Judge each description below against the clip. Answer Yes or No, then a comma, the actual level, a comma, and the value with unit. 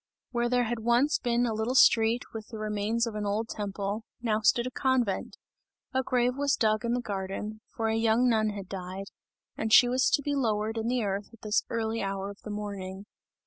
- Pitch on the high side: Yes, high, 220 Hz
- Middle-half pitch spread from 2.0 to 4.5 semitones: Yes, narrow, 2.5 semitones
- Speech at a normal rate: No, fast, 215 wpm